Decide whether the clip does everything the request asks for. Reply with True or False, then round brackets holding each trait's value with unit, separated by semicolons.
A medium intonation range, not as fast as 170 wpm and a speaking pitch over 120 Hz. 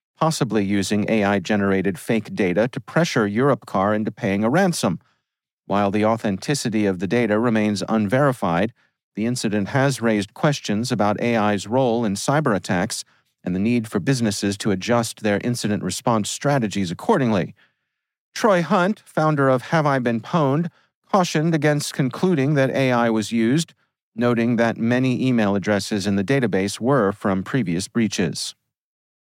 False (4.6 semitones; 140 wpm; 115 Hz)